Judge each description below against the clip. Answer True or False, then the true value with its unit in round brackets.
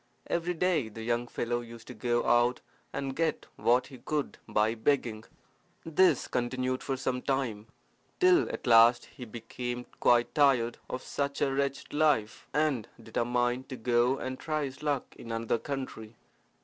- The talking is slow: False (160 wpm)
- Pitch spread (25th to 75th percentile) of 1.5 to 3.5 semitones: True (3.0 semitones)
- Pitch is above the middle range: False (125 Hz)